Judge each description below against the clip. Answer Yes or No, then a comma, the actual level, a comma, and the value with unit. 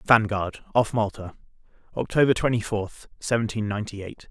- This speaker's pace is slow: Yes, slow, 125 wpm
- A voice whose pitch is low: Yes, low, 110 Hz